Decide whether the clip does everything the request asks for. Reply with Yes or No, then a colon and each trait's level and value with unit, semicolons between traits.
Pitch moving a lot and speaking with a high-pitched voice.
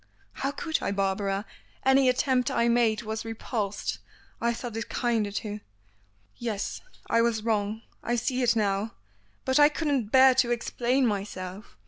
No: average, 3.4 semitones; high, 230 Hz